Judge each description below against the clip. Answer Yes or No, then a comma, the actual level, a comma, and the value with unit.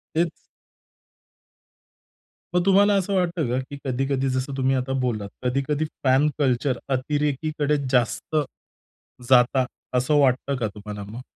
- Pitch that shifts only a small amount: No, average, 3.0 semitones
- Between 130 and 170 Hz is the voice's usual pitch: Yes, low, 135 Hz